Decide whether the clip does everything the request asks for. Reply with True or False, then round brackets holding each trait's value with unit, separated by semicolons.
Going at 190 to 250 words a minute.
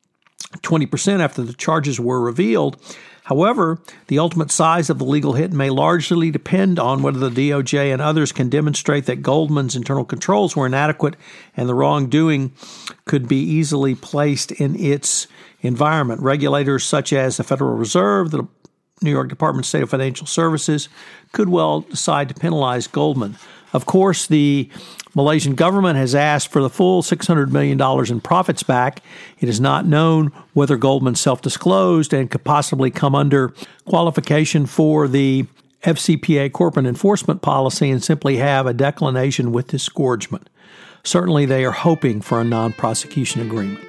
False (155 wpm)